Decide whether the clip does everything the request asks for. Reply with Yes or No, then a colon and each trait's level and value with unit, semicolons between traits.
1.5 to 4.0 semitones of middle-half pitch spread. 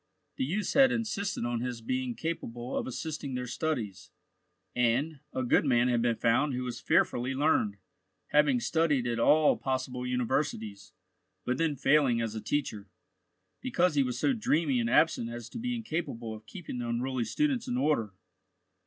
No: average, 4.6 semitones